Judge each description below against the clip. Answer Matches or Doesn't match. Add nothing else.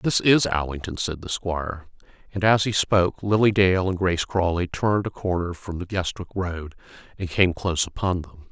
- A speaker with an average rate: Matches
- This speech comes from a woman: Doesn't match